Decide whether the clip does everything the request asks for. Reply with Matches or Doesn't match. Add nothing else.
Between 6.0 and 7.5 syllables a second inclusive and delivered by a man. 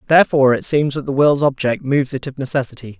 Matches